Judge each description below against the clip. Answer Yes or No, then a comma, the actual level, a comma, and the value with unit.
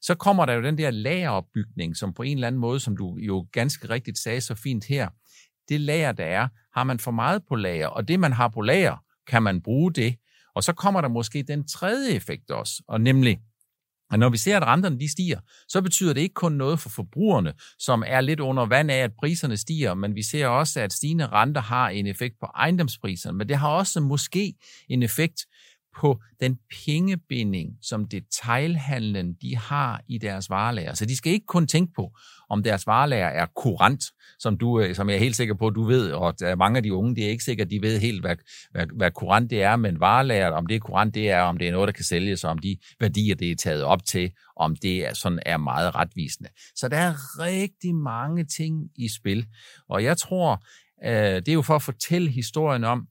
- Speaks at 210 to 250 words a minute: Yes, average, 220 wpm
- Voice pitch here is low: Yes, low, 120 Hz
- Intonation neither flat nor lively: No, wide, 6.2 semitones